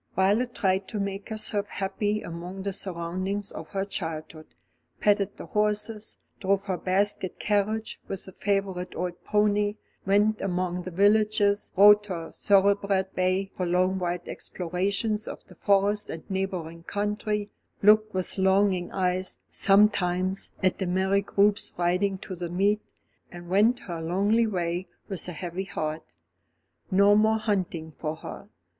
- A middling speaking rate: Yes, average, 145 wpm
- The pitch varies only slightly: Yes, narrow, 2.3 semitones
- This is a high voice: Yes, high, 195 Hz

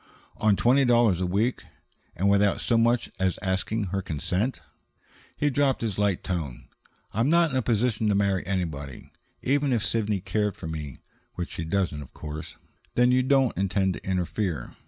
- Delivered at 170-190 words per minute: Yes, average, 175 wpm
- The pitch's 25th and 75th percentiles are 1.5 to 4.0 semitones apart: No, average, 4.7 semitones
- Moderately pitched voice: No, low, 100 Hz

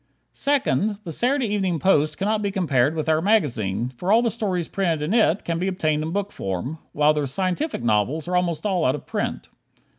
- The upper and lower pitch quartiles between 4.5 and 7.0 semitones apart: Yes, average, 5.1 semitones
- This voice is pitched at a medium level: Yes, medium, 170 Hz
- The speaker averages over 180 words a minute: Yes, fast, 205 wpm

